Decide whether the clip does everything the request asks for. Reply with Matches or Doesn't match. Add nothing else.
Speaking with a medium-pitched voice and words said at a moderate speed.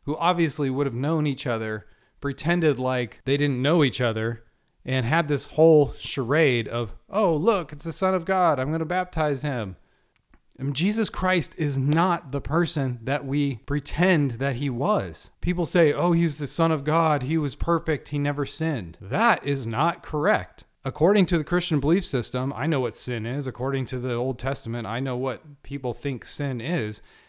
Matches